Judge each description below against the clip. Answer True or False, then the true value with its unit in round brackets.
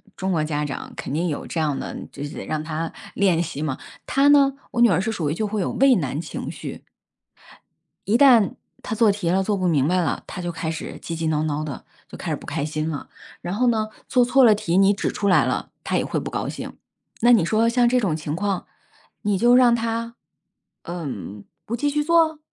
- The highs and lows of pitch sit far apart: True (6.7 semitones)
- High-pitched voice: True (195 Hz)